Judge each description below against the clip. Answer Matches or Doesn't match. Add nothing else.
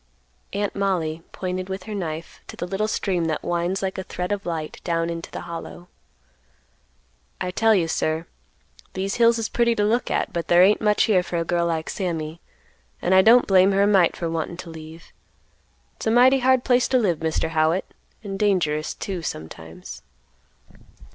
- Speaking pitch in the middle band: Matches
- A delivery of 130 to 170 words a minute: Doesn't match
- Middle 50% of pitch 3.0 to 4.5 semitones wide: Matches